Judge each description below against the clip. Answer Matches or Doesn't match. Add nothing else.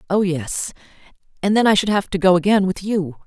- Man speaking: Doesn't match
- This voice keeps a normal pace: Doesn't match